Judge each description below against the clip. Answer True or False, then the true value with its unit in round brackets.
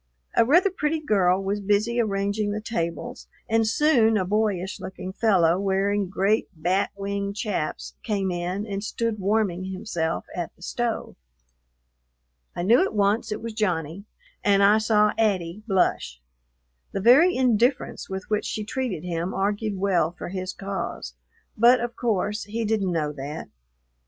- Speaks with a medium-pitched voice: False (200 Hz)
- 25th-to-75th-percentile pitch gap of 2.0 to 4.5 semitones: True (2.9 semitones)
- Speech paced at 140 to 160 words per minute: True (150 wpm)